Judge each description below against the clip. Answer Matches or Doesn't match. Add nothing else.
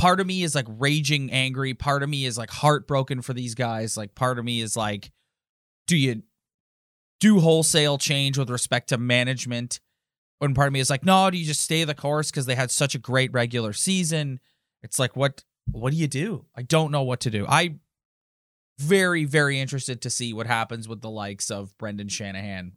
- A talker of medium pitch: Doesn't match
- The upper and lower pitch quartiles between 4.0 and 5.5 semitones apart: Matches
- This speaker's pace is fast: Matches